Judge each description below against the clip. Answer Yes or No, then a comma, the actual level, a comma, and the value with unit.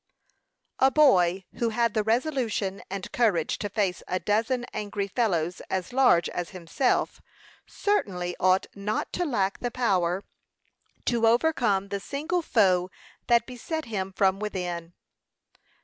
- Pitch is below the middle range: No, high, 205 Hz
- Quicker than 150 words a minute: No, slow, 135 wpm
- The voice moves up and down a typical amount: Yes, average, 4.7 semitones